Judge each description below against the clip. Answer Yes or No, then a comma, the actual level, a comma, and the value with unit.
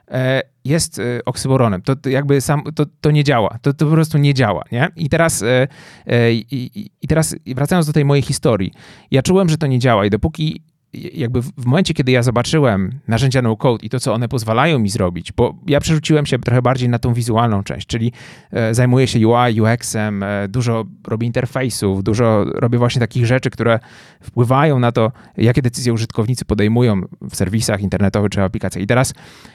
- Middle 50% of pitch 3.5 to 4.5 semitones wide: Yes, average, 3.9 semitones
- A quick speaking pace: Yes, fast, 180 wpm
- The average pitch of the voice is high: No, low, 125 Hz